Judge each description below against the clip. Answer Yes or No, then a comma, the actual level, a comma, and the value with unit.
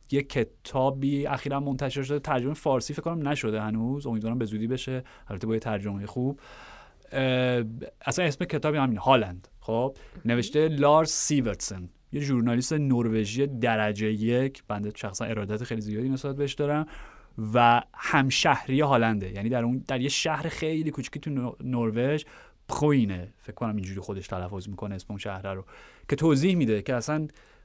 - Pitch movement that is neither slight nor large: Yes, average, 4.4 semitones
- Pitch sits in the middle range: No, low, 125 Hz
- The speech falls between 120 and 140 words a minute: No, fast, 155 wpm